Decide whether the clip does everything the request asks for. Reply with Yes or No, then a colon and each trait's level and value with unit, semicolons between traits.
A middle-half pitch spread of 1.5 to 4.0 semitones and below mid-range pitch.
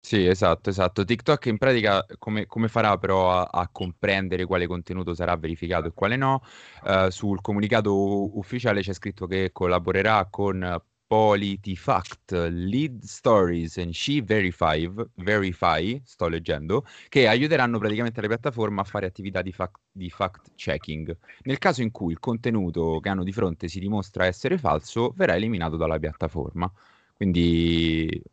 Yes: average, 3.5 semitones; very low, 95 Hz